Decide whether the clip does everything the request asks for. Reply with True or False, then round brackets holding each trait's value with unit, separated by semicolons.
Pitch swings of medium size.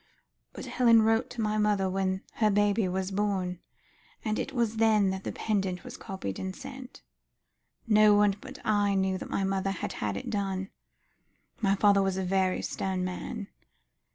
False (2.1 semitones)